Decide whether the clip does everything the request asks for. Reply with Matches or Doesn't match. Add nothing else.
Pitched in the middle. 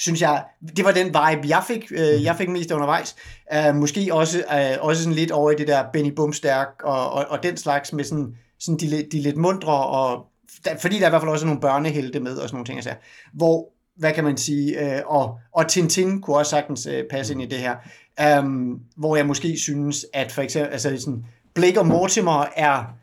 Matches